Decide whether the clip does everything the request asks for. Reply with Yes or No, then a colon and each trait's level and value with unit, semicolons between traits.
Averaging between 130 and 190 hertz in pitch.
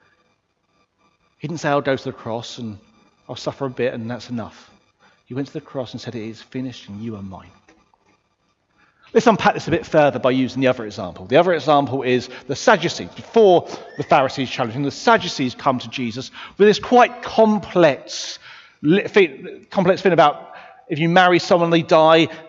Yes: low, 135 Hz